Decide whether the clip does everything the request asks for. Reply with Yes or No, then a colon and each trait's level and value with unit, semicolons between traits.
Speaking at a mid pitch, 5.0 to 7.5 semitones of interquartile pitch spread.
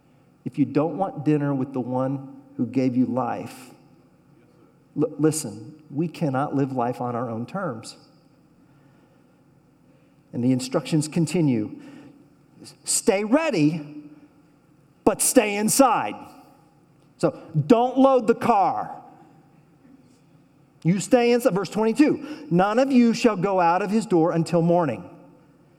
Yes: medium, 155 Hz; wide, 5.4 semitones